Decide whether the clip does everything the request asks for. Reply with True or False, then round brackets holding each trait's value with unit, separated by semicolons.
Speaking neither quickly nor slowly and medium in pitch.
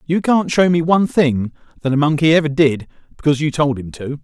False (225 wpm; 150 Hz)